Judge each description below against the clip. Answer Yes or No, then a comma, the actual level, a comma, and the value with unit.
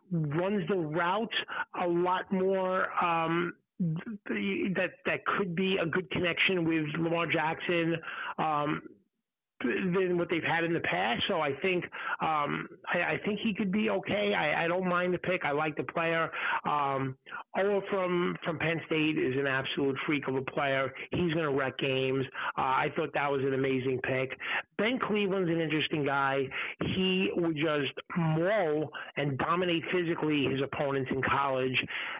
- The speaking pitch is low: No, medium, 165 Hz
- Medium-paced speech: Yes, average, 165 wpm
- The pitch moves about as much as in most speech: Yes, average, 4.5 semitones